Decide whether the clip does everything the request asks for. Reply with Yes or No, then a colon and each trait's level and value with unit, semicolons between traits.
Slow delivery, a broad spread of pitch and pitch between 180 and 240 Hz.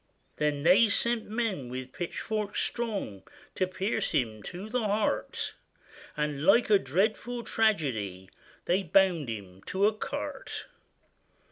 Yes: slow, 125 wpm; wide, 7.7 semitones; high, 190 Hz